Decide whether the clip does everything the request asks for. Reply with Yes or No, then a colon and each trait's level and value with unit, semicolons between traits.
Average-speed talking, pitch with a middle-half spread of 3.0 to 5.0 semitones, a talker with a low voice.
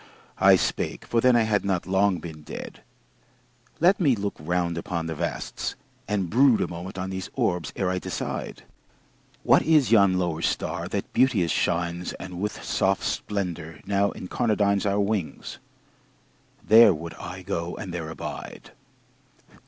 Yes: average, 150 wpm; average, 3.3 semitones; very low, 95 Hz